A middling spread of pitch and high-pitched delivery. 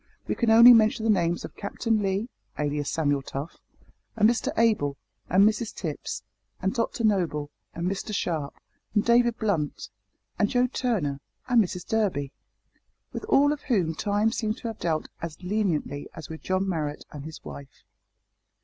No: wide, 6.3 semitones; high, 195 Hz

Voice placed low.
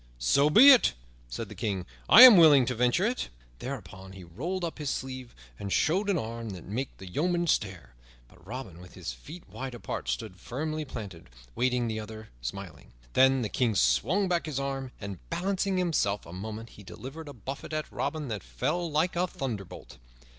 Yes: low, 125 Hz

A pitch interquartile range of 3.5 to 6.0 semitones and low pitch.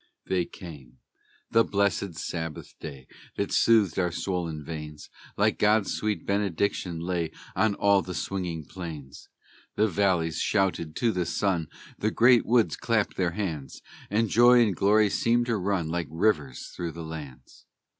Yes: average, 4.3 semitones; very low, 90 Hz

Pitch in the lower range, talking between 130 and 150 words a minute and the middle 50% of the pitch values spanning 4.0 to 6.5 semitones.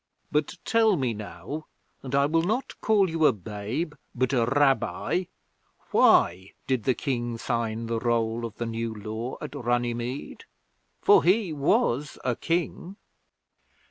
Yes: low, 125 Hz; average, 140 wpm; average, 5.1 semitones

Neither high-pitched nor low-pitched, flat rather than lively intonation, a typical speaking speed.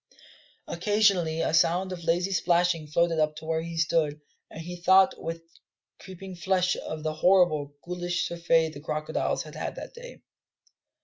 Yes: medium, 170 Hz; narrow, 2.2 semitones; average, 160 wpm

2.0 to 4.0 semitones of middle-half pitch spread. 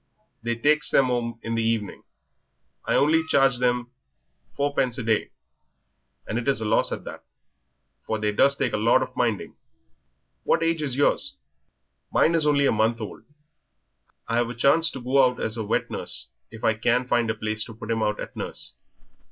Yes: average, 3.7 semitones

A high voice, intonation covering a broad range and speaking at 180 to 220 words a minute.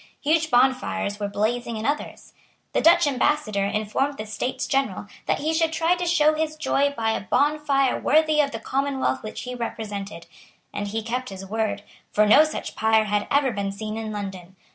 Yes: high, 240 Hz; wide, 5.7 semitones; average, 185 wpm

